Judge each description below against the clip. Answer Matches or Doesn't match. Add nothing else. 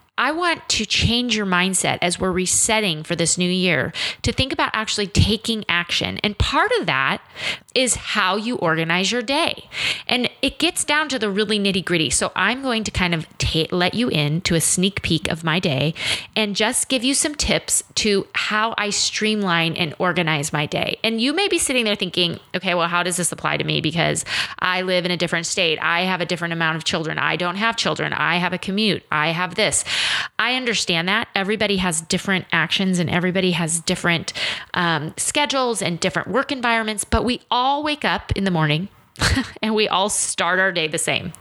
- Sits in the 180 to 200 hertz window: Matches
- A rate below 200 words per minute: Doesn't match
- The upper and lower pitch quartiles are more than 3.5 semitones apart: Matches